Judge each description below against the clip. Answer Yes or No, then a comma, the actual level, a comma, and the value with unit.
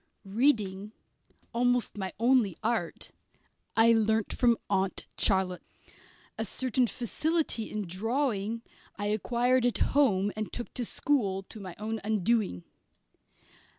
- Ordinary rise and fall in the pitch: Yes, average, 3.6 semitones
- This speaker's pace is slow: Yes, slow, 115 wpm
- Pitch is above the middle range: Yes, high, 220 Hz